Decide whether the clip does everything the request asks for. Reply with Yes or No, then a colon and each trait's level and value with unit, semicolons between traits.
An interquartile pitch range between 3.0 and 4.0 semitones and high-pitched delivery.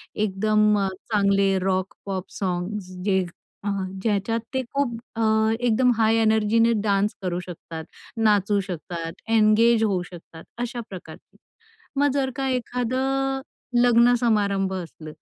Yes: average, 3.7 semitones; high, 210 Hz